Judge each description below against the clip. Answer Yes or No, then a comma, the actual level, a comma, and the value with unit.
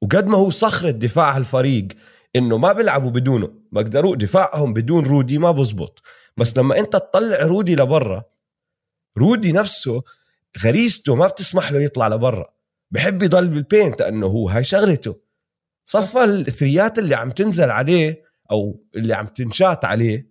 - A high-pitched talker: No, medium, 145 Hz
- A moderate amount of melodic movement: No, wide, 8.3 semitones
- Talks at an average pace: No, fast, 140 wpm